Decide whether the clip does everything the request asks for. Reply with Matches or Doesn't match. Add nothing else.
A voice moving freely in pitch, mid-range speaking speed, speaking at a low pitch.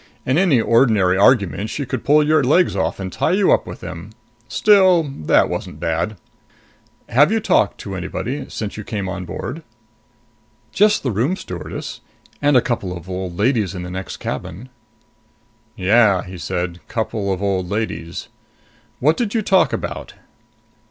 Matches